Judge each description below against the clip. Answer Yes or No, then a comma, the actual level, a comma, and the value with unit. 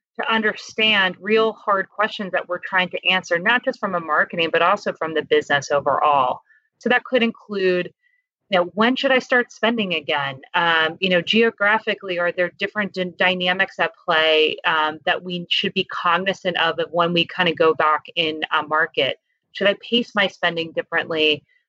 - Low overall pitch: No, medium, 180 Hz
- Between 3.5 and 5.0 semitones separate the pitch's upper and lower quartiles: Yes, average, 4.2 semitones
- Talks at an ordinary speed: Yes, average, 185 wpm